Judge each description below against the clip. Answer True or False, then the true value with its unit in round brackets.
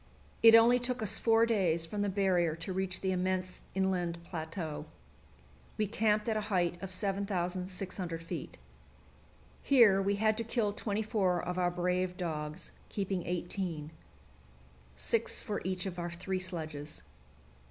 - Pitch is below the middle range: False (185 Hz)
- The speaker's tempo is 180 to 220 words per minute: False (145 wpm)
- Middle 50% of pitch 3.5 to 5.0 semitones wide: False (2.9 semitones)